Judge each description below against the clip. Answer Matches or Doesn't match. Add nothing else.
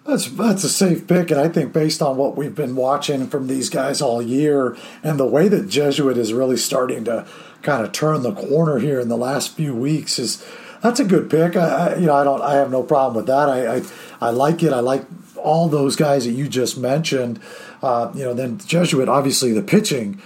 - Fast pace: Matches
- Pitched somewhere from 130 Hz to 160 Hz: Matches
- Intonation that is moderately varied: Matches